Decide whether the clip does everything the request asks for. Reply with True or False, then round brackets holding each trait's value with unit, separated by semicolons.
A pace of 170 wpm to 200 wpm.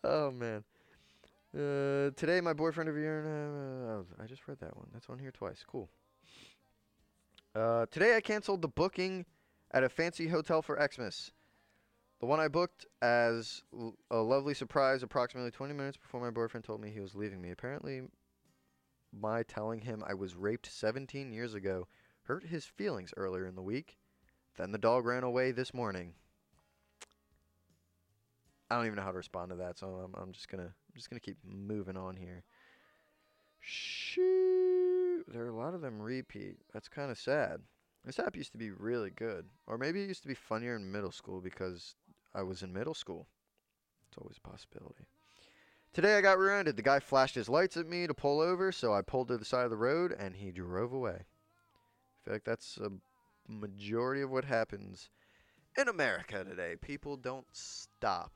True (185 wpm)